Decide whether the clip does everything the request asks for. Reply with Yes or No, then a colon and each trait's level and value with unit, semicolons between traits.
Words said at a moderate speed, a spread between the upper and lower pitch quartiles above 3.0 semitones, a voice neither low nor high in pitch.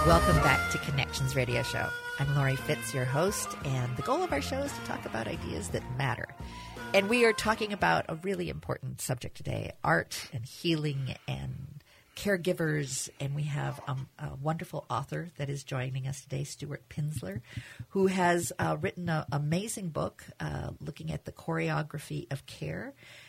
Yes: average, 175 wpm; average, 4.2 semitones; medium, 145 Hz